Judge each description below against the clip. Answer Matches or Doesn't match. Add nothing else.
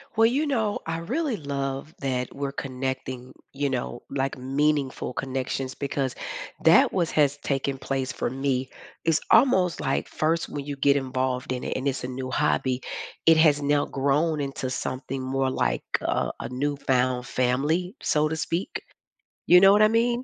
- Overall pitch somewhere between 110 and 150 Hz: Matches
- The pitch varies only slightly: Doesn't match